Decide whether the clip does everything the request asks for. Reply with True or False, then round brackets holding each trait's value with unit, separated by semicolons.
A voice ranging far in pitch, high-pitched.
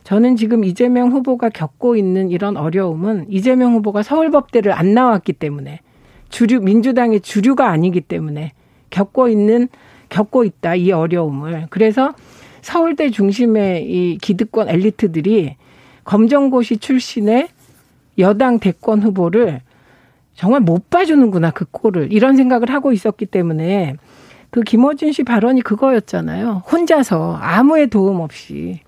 True (5.8 semitones; 215 Hz)